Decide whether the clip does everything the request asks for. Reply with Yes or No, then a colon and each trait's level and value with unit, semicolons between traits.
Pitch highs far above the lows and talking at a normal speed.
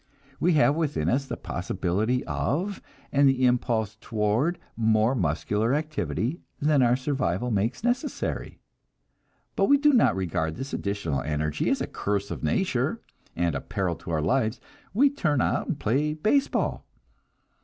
Yes: wide, 7.3 semitones; average, 150 wpm